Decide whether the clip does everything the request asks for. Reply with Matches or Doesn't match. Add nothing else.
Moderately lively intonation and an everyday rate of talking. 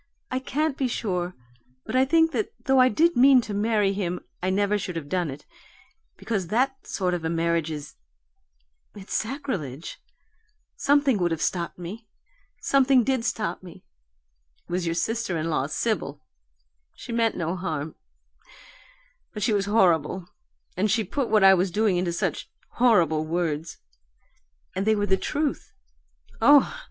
Doesn't match